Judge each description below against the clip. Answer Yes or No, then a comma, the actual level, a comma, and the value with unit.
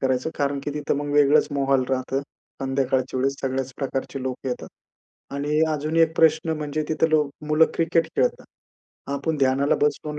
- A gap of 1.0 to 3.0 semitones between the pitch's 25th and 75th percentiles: Yes, narrow, 2.5 semitones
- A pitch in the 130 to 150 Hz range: Yes, medium, 140 Hz